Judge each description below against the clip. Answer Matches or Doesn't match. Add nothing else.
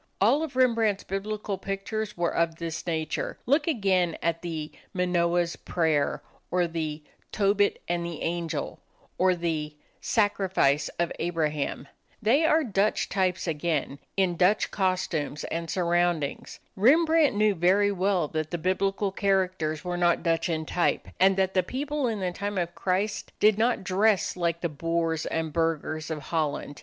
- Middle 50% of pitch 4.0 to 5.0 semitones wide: Doesn't match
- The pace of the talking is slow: Doesn't match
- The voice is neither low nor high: Matches